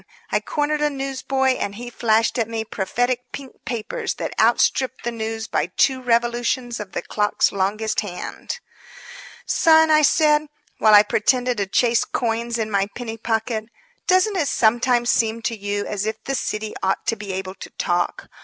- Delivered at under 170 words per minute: No, average, 175 wpm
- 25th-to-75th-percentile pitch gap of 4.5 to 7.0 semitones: No, average, 3.3 semitones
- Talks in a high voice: Yes, high, 230 Hz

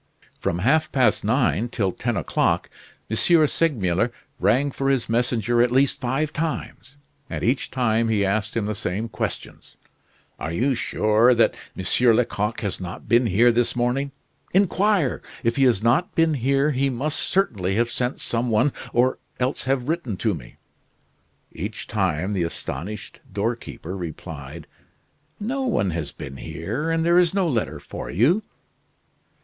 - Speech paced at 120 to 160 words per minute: Yes, average, 155 wpm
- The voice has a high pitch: No, low, 120 Hz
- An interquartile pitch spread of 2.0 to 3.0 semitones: No, average, 5.0 semitones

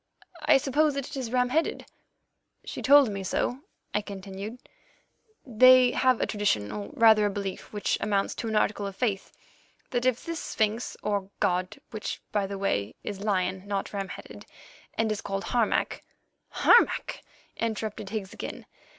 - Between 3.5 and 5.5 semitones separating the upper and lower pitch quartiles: Yes, average, 3.9 semitones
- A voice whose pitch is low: No, high, 210 Hz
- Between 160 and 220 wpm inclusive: Yes, average, 165 wpm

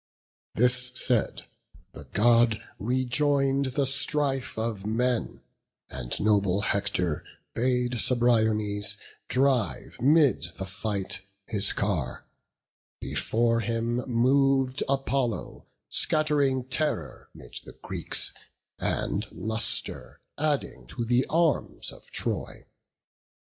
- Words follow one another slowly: Yes, slow, 95 wpm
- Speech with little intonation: No, average, 3.9 semitones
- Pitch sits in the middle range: No, low, 120 Hz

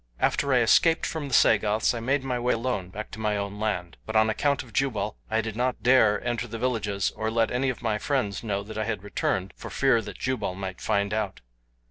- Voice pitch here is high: No, low, 110 Hz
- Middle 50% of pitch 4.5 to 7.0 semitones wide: No, average, 3.3 semitones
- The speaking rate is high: Yes, fast, 230 wpm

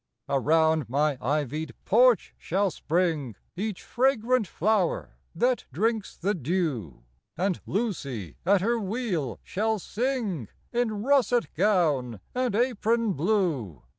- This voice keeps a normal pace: No, slow, 110 wpm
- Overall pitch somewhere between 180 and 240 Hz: Yes, high, 190 Hz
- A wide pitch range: Yes, wide, 6.9 semitones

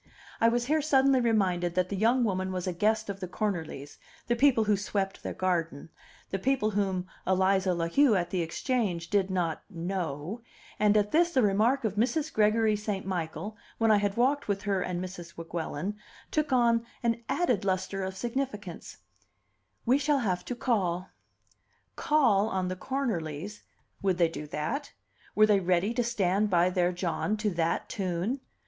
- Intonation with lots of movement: No, average, 4.3 semitones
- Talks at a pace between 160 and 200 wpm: Yes, average, 175 wpm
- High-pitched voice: Yes, high, 200 Hz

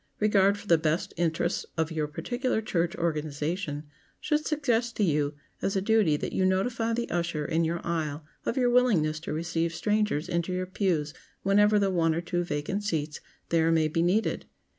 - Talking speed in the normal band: Yes, average, 185 wpm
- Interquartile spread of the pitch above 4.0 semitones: Yes, average, 4.5 semitones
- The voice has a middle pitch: Yes, medium, 170 Hz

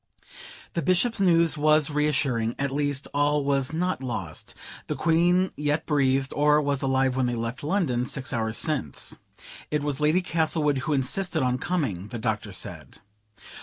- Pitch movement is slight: No, average, 3.6 semitones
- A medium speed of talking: Yes, average, 160 wpm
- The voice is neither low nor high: Yes, medium, 145 Hz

